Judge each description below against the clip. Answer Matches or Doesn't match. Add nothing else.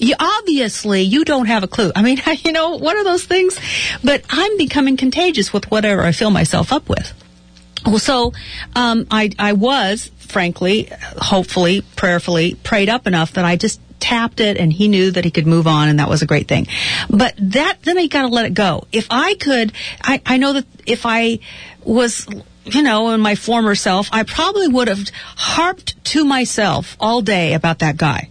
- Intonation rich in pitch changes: Matches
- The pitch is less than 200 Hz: Doesn't match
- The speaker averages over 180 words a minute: Matches